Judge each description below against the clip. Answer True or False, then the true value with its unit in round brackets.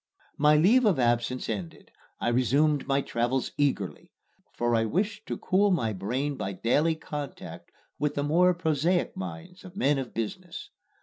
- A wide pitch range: True (6.0 semitones)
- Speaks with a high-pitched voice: False (145 Hz)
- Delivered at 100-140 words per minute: False (160 wpm)